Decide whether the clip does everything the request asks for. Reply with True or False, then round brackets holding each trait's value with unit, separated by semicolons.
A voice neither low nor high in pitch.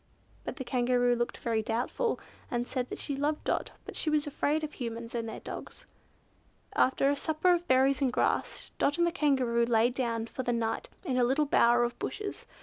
False (255 Hz)